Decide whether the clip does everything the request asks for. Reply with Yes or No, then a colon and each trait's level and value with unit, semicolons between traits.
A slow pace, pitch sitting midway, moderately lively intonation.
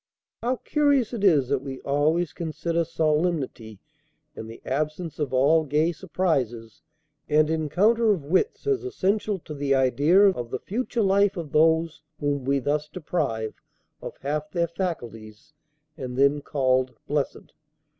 No: average, 145 wpm; medium, 155 Hz; average, 4.6 semitones